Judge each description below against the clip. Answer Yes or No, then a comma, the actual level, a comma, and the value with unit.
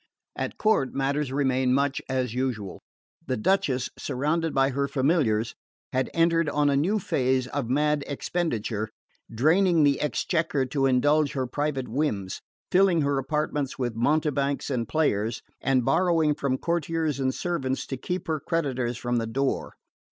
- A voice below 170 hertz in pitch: Yes, medium, 140 Hz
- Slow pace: No, average, 150 wpm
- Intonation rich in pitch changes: No, average, 3.3 semitones